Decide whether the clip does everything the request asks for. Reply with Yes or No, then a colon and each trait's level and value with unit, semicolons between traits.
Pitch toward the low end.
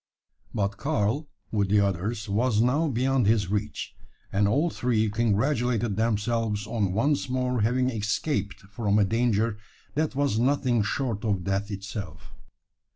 Yes: low, 110 Hz